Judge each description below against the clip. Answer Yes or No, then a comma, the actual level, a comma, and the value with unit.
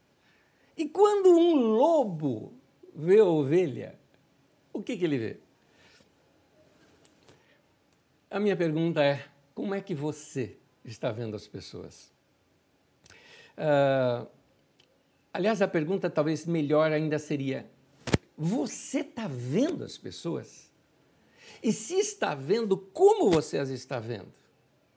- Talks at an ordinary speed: No, slow, 110 wpm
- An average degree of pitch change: No, wide, 7.8 semitones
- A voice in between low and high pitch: Yes, medium, 160 Hz